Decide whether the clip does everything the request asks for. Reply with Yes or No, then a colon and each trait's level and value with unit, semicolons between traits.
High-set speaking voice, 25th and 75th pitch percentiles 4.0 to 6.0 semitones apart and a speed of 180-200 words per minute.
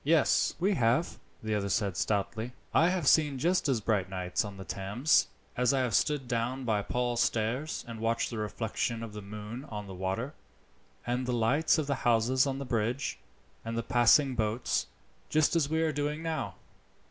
No: low, 120 Hz; average, 4.6 semitones; average, 185 wpm